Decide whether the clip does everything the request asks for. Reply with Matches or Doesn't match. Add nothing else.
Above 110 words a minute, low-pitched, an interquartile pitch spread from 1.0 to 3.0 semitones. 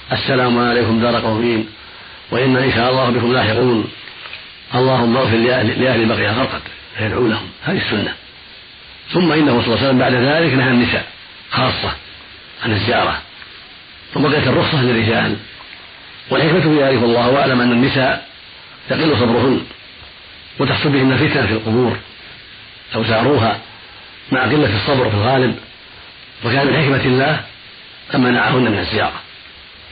Matches